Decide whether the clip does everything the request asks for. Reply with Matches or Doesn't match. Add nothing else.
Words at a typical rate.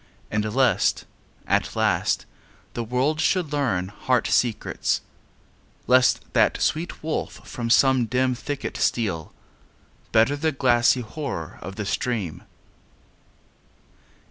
Doesn't match